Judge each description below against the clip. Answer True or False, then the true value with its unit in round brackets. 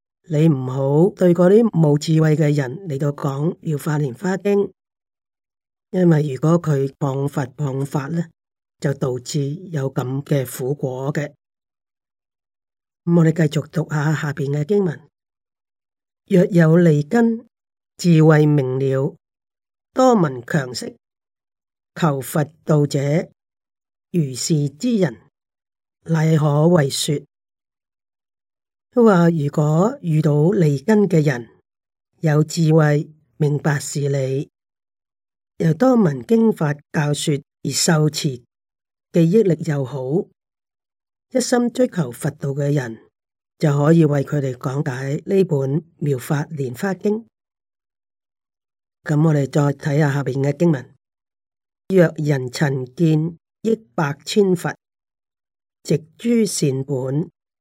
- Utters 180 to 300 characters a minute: False (160 characters per minute)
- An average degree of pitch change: True (3.3 semitones)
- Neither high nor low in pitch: True (150 Hz)